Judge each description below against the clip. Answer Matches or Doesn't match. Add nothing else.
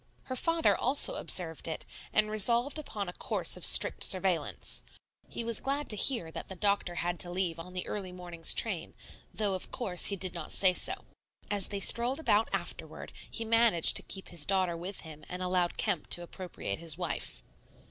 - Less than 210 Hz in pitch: Matches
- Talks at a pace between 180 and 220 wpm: Matches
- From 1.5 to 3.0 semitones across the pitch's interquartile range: Doesn't match